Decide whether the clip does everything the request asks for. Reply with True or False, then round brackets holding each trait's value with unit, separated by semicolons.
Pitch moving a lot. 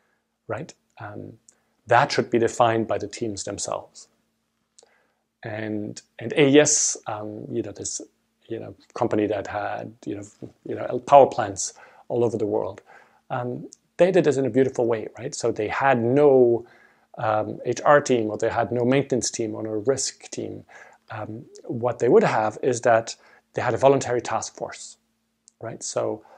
False (2.7 semitones)